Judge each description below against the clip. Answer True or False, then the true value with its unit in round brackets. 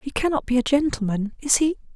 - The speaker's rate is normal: True (185 wpm)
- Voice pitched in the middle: False (265 Hz)